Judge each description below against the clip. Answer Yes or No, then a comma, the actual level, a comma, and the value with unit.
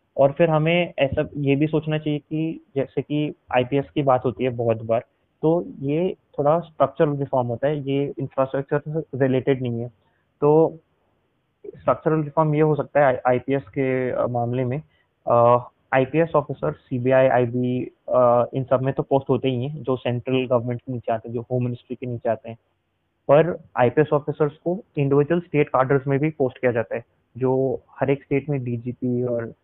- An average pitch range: Yes, average, 3.2 semitones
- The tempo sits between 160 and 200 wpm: Yes, average, 180 wpm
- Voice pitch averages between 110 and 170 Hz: Yes, low, 135 Hz